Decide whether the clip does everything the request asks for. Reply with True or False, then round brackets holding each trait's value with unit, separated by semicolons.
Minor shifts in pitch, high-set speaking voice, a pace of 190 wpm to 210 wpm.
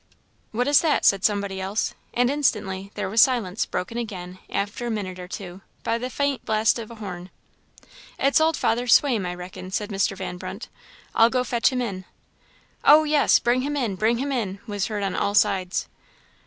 False (4.4 semitones; 215 Hz; 195 wpm)